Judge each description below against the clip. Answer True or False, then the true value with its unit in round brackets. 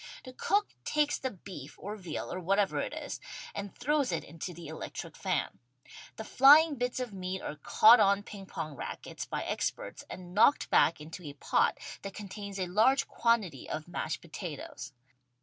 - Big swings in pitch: True (5.8 semitones)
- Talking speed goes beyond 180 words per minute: False (175 wpm)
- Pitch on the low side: False (195 Hz)